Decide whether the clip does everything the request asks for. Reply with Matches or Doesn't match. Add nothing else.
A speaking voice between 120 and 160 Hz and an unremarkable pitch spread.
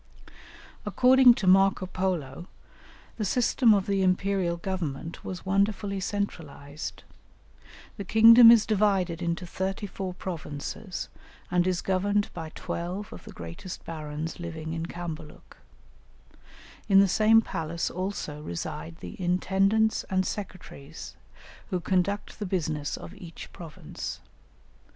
Doesn't match